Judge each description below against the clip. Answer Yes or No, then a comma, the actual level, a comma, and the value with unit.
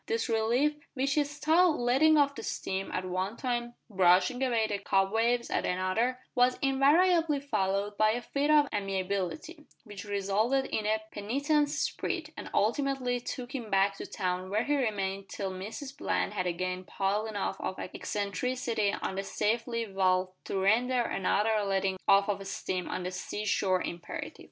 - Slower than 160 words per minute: No, average, 165 wpm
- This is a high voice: Yes, high, 215 Hz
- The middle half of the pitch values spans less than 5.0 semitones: No, wide, 5.4 semitones